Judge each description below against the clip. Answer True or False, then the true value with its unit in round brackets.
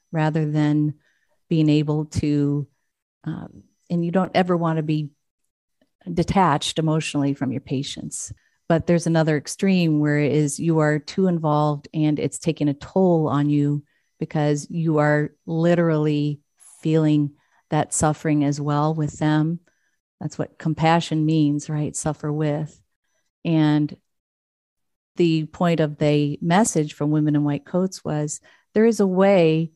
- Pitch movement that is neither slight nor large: False (1.9 semitones)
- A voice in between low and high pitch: True (155 Hz)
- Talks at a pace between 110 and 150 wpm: True (140 wpm)